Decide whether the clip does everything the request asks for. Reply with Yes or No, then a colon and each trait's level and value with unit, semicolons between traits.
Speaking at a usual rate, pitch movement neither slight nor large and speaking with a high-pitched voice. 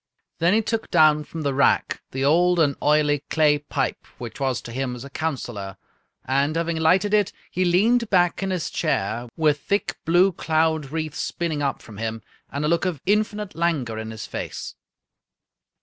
No: average, 180 wpm; average, 4.6 semitones; medium, 155 Hz